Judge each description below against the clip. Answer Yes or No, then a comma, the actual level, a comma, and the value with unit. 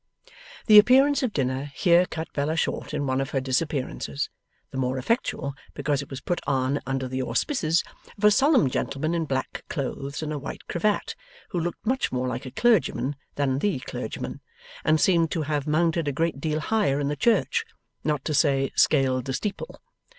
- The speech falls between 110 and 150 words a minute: No, average, 185 wpm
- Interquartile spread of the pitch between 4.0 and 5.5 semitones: Yes, average, 4.3 semitones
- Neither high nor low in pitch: Yes, medium, 150 Hz